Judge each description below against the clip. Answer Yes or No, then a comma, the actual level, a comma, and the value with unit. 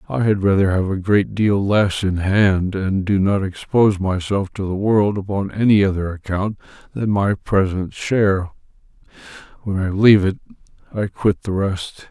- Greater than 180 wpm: No, average, 170 wpm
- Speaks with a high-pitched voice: No, low, 100 Hz